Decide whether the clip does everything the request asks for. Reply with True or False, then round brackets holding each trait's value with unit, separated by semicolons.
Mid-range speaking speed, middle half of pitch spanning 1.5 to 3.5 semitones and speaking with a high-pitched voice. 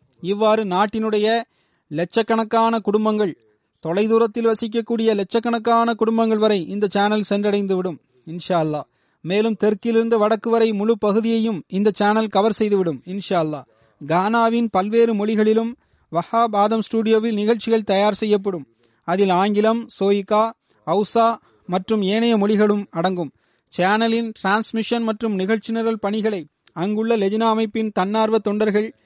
True (110 wpm; 2.7 semitones; 215 Hz)